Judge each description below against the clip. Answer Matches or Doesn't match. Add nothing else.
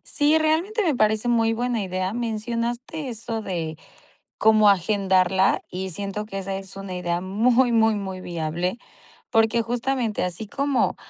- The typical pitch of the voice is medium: Doesn't match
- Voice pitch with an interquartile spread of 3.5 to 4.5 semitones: Matches